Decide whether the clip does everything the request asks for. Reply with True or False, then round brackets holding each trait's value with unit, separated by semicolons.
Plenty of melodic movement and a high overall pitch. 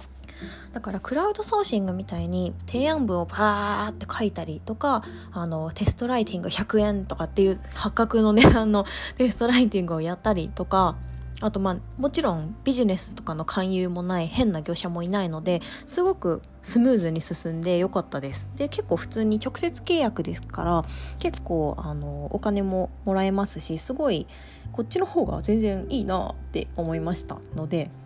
True (6.0 semitones; 195 Hz)